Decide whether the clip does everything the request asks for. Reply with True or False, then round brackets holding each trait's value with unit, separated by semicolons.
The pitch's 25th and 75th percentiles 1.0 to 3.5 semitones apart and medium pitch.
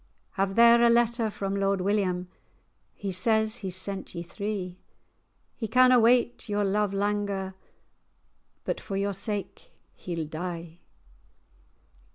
False (2.8 semitones; 200 Hz)